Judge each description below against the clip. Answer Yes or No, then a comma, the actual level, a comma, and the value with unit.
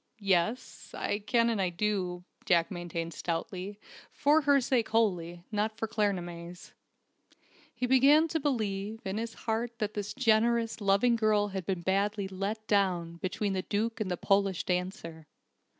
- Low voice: No, high, 205 Hz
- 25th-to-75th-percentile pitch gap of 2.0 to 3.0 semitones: No, average, 3.8 semitones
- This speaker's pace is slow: No, average, 150 wpm